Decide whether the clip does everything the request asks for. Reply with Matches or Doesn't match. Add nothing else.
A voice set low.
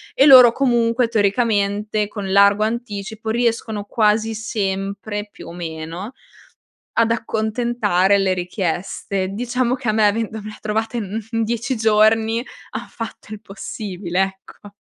Doesn't match